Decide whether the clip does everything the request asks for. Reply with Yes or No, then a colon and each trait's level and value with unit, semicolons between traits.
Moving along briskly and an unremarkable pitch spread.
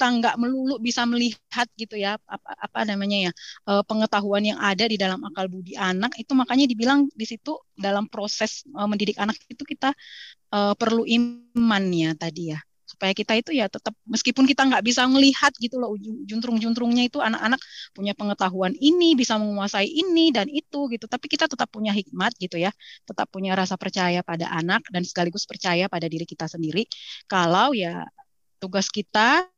Yes: fast, 165 wpm; average, 4.2 semitones